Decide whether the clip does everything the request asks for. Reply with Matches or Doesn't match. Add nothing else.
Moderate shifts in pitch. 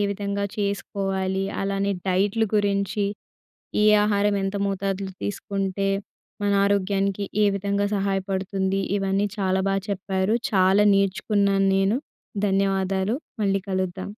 Doesn't match